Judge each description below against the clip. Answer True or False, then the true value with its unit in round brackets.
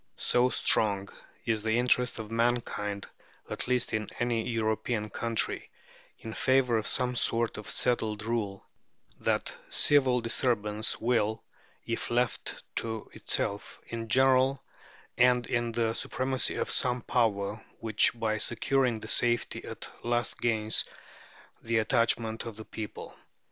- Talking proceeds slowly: True (130 wpm)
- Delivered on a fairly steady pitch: True (2.0 semitones)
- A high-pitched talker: False (115 Hz)